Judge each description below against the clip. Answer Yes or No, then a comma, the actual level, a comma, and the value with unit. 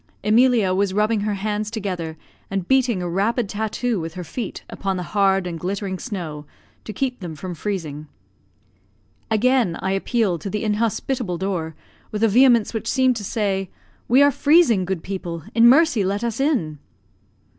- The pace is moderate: Yes, average, 165 wpm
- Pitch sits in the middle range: No, high, 205 Hz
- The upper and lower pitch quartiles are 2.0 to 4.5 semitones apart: Yes, average, 4.0 semitones